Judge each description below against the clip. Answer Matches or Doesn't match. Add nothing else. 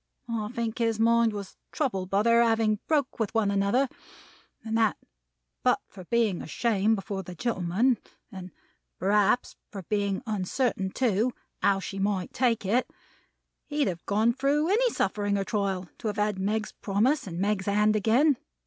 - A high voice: Matches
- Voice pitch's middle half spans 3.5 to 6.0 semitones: Doesn't match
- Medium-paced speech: Matches